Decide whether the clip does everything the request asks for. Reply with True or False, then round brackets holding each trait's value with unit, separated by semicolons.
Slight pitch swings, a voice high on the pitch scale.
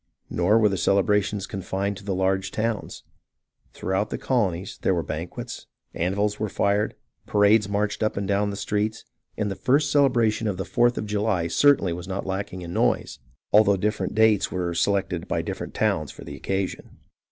False (2.1 semitones; 100 Hz)